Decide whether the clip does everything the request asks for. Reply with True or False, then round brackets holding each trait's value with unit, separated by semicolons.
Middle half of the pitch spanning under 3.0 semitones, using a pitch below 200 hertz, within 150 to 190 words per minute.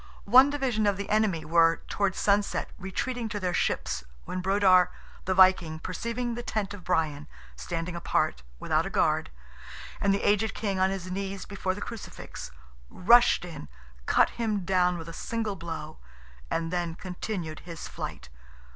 False (3.4 semitones; 190 Hz; 160 wpm)